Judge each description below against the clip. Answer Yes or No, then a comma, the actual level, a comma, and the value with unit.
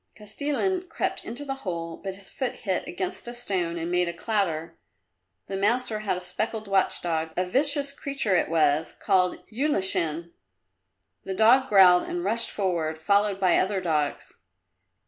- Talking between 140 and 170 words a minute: Yes, average, 160 wpm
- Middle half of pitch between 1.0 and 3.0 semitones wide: No, average, 5.2 semitones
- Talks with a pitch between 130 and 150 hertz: No, high, 195 Hz